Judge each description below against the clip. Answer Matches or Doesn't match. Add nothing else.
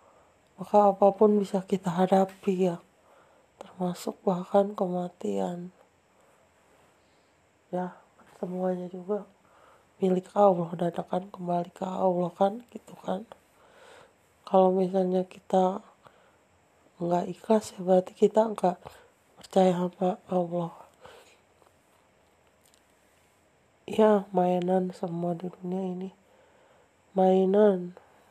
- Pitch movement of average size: Doesn't match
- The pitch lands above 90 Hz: Matches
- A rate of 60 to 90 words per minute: Matches